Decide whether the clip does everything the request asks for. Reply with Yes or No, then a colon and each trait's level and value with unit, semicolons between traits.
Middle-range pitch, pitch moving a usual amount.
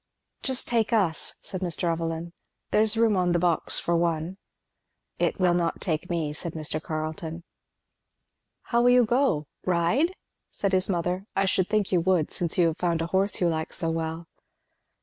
Yes: medium, 175 Hz; average, 3.0 semitones